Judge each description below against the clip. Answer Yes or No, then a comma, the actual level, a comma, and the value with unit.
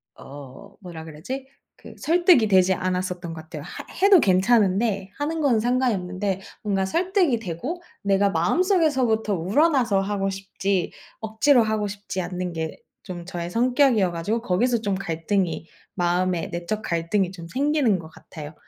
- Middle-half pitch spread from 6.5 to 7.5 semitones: No, wide, 5.4 semitones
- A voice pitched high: Yes, high, 195 Hz